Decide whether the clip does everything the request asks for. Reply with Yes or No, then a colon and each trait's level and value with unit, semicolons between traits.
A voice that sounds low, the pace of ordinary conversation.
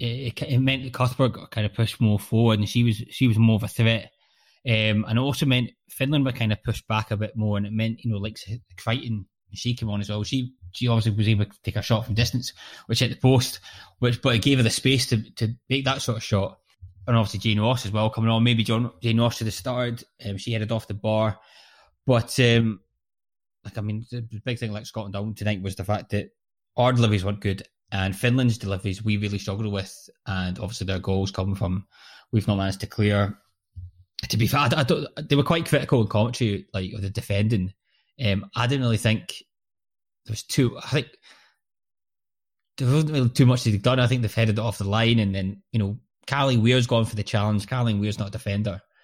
No: low, 110 Hz; fast, 235 wpm